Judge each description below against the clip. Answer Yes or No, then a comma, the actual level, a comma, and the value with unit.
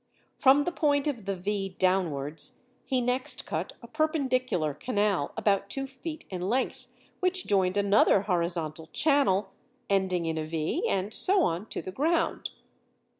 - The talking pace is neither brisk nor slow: Yes, average, 150 wpm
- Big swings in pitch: Yes, wide, 7.1 semitones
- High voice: Yes, high, 200 Hz